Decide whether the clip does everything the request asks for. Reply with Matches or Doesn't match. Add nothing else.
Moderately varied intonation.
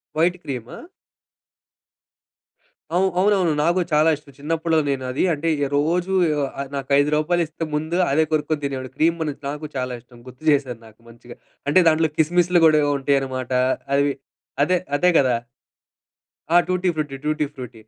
Matches